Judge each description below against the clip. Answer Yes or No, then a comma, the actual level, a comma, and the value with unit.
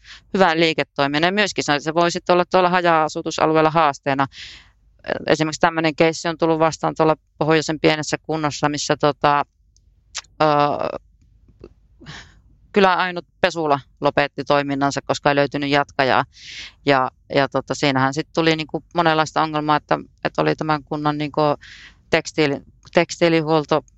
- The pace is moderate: Yes, average, 125 wpm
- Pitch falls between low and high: Yes, medium, 150 Hz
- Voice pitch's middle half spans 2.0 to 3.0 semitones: Yes, narrow, 2.5 semitones